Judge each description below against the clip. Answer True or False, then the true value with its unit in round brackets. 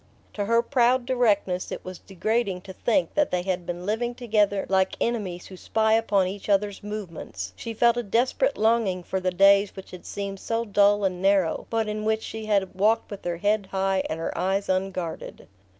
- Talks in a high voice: True (200 Hz)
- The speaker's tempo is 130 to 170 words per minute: False (200 wpm)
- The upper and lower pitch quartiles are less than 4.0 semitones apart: True (2.9 semitones)